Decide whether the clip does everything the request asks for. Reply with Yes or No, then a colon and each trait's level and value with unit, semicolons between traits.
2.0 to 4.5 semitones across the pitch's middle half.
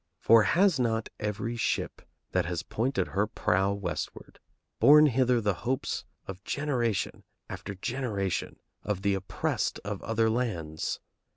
Yes: average, 4.1 semitones